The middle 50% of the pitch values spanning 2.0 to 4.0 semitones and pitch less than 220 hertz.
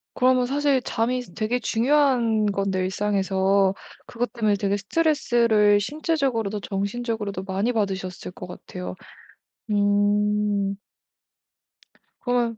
Yes: average, 3.6 semitones; high, 210 Hz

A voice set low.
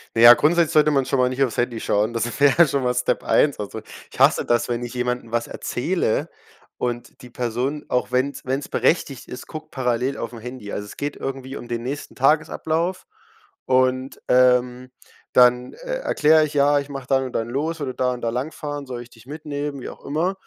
Yes: low, 130 Hz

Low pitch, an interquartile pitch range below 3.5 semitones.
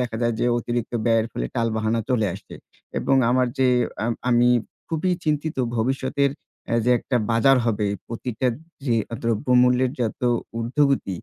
Yes: low, 120 Hz; narrow, 2.4 semitones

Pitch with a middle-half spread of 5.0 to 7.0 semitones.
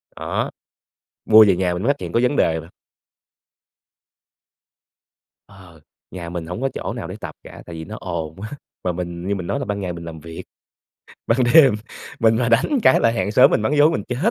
Yes: average, 5.3 semitones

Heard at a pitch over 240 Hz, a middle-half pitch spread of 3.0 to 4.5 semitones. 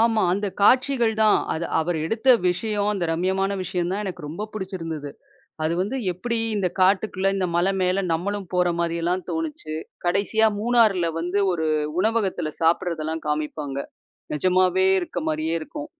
No: medium, 185 Hz; average, 3.7 semitones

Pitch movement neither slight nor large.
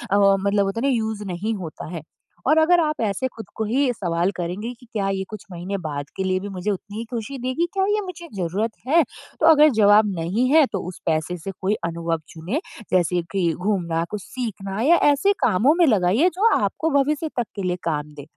No: wide, 6.4 semitones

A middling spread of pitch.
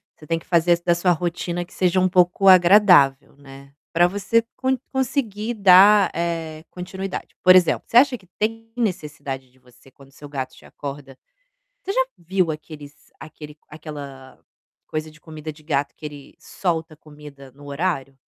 Yes: average, 4.4 semitones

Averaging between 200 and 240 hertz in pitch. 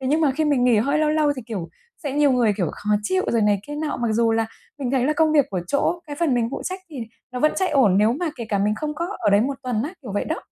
No: very high, 260 Hz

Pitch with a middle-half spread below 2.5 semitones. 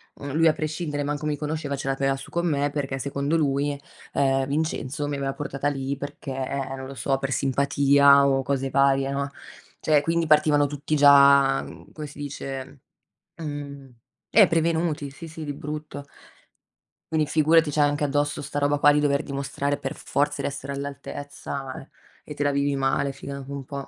Yes: narrow, 1.2 semitones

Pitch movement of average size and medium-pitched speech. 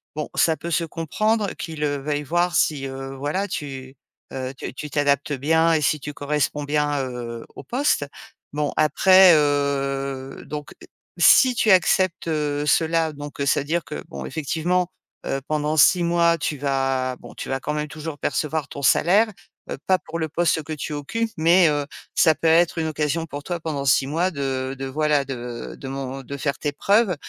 Yes: average, 3.1 semitones; medium, 150 Hz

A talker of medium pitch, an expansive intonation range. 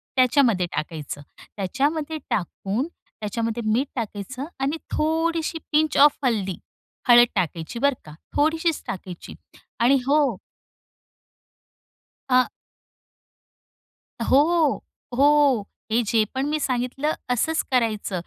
No: very high, 255 Hz; wide, 5.7 semitones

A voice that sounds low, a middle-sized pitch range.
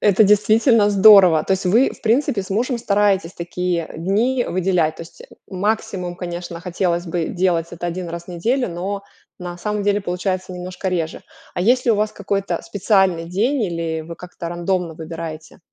No: medium, 185 Hz; average, 3.1 semitones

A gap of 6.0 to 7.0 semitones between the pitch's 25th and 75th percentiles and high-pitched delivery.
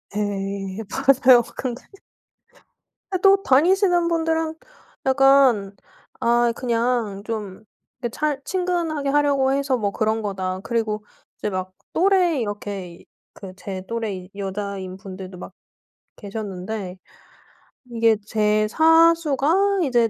Yes: wide, 6.6 semitones; high, 230 Hz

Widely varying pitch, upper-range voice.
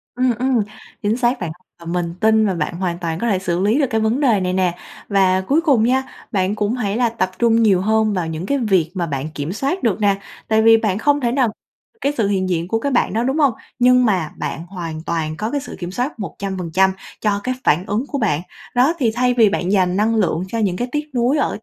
No: average, 4.9 semitones; high, 210 Hz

